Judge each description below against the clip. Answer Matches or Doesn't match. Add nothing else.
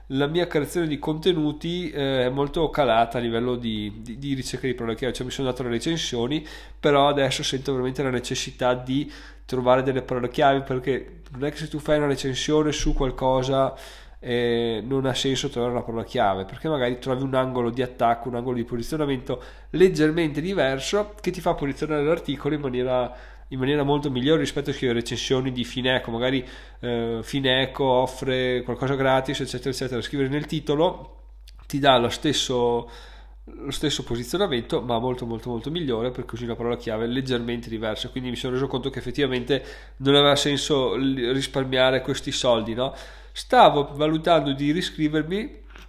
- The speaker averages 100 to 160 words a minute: Doesn't match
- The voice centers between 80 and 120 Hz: Doesn't match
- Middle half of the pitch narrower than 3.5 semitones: Matches